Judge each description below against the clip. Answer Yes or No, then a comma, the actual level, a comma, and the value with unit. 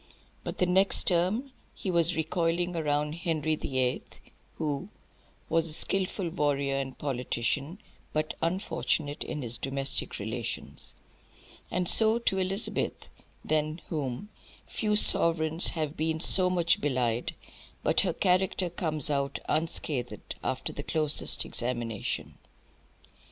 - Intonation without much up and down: No, average, 4.3 semitones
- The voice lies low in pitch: No, medium, 155 Hz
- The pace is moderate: No, slow, 120 wpm